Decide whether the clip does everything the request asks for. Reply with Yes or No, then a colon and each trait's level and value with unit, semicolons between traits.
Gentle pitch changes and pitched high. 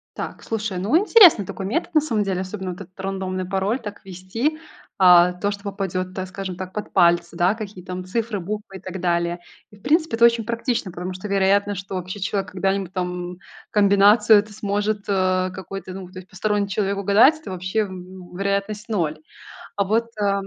Yes: narrow, 2.2 semitones; high, 195 Hz